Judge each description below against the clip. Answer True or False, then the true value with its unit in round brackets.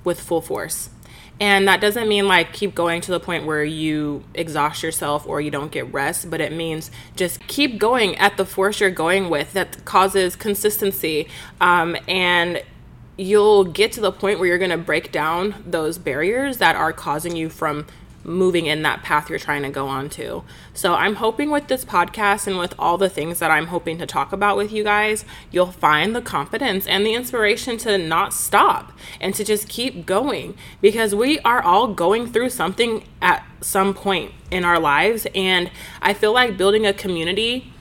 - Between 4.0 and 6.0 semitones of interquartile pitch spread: True (4.3 semitones)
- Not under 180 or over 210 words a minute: True (190 wpm)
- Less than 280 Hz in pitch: True (185 Hz)